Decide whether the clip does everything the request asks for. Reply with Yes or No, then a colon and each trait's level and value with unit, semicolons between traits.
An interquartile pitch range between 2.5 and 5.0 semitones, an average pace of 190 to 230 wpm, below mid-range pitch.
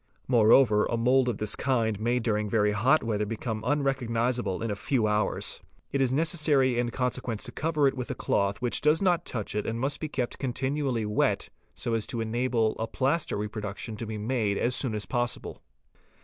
Yes: average, 3.5 semitones; average, 195 wpm; low, 120 Hz